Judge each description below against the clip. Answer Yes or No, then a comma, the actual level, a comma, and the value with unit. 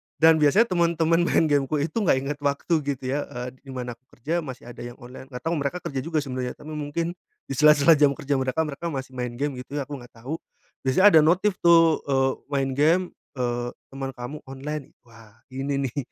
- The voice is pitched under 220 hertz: Yes, medium, 140 Hz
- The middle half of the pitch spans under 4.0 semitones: Yes, average, 3.3 semitones